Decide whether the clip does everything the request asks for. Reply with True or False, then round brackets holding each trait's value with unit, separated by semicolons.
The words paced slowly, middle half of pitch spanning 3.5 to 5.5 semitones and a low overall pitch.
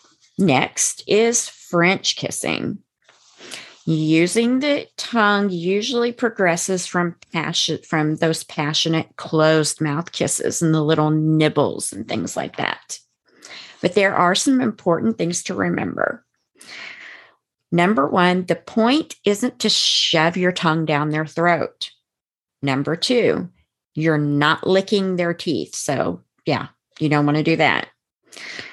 False (125 wpm; 4.5 semitones; 170 Hz)